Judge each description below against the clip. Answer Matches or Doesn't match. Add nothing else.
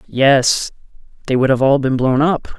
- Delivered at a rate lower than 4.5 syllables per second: Matches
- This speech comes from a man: Matches